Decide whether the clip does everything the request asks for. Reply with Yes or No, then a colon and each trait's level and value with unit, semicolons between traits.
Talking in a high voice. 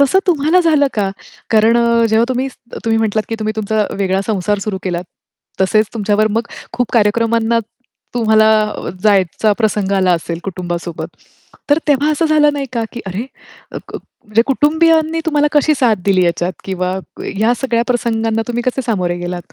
Yes: high, 225 Hz